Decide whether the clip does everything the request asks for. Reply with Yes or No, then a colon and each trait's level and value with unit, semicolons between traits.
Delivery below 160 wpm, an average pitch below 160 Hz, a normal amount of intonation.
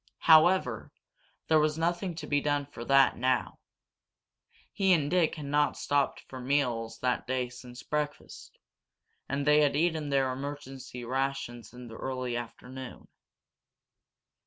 Yes: slow, 135 wpm; medium, 140 Hz; average, 3.1 semitones